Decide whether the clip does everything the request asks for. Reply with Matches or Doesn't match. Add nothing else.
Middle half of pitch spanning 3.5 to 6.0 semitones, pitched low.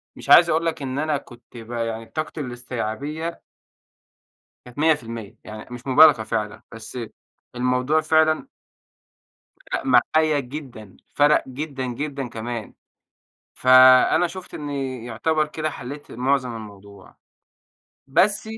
Matches